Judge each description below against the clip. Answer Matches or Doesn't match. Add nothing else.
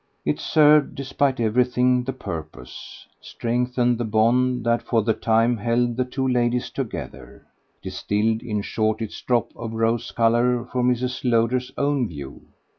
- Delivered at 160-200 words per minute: Doesn't match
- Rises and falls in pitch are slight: Matches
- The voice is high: Doesn't match